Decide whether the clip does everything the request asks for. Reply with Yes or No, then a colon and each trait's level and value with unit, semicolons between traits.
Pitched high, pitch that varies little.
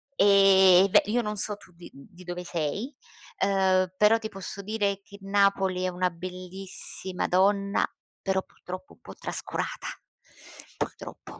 Yes: high, 195 Hz; narrow, 1.6 semitones